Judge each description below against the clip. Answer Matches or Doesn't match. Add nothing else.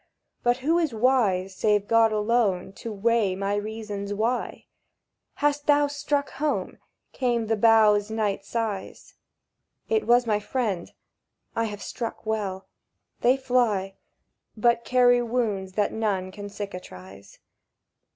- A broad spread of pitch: Doesn't match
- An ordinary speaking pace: Doesn't match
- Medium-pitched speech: Doesn't match